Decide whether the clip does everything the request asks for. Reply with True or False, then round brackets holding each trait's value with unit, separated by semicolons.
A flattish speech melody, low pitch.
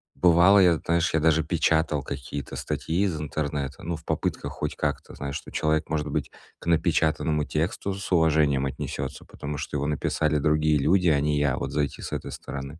True (2.2 semitones; 75 Hz)